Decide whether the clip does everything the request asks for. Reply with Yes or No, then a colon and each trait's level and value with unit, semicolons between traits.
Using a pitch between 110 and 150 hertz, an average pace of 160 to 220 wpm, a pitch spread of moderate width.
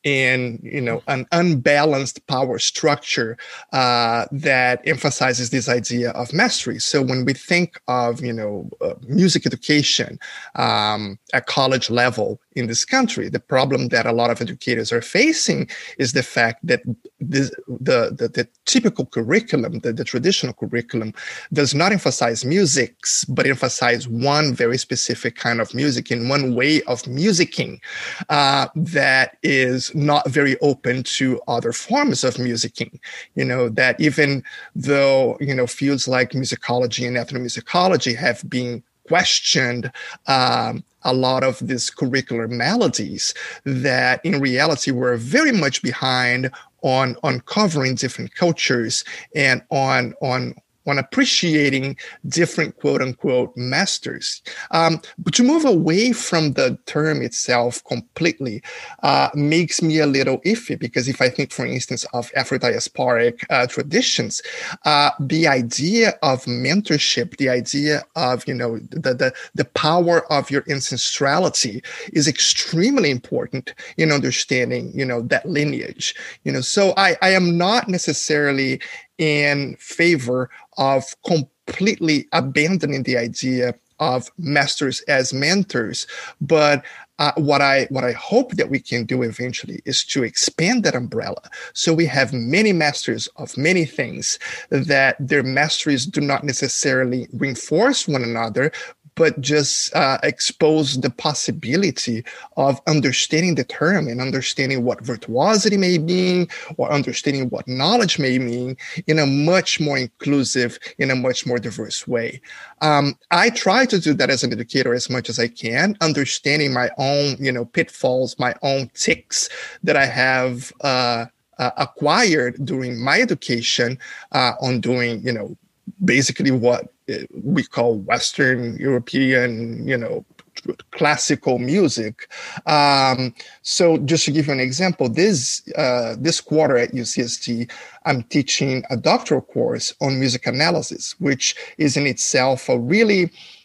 No: low, 135 Hz; average, 140 wpm; average, 3.9 semitones